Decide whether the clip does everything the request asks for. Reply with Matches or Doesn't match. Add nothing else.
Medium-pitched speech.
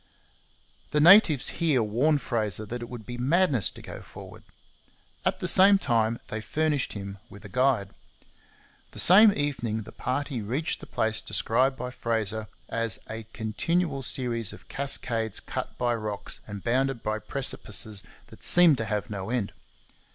Doesn't match